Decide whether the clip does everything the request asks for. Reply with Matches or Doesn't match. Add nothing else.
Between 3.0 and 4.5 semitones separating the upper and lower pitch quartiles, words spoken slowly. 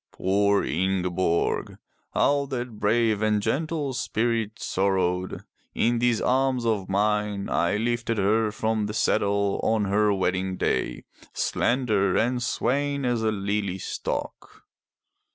Matches